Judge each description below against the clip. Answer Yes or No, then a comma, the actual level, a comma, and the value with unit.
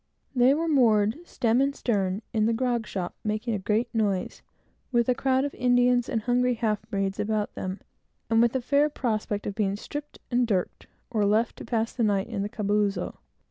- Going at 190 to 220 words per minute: Yes, average, 195 wpm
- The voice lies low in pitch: No, high, 225 Hz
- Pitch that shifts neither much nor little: Yes, average, 3.1 semitones